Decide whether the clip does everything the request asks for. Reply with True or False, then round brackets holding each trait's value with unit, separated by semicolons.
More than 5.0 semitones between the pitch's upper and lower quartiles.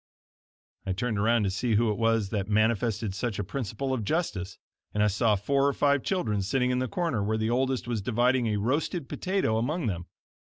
False (4.1 semitones)